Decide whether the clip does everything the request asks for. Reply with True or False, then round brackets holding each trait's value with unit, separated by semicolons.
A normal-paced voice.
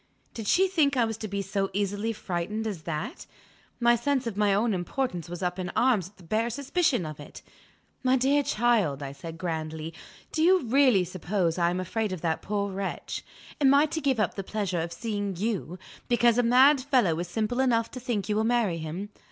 False (210 wpm)